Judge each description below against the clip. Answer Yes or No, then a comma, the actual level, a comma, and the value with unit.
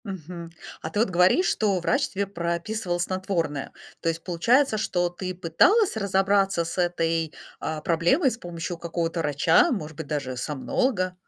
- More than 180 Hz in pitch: No, medium, 175 Hz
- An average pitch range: Yes, average, 3.2 semitones